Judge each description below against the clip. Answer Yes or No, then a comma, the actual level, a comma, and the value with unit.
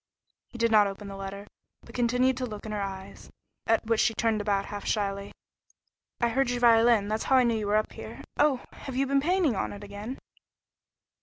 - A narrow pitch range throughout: No, average, 3.4 semitones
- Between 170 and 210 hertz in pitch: No, high, 225 Hz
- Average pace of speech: No, fast, 215 wpm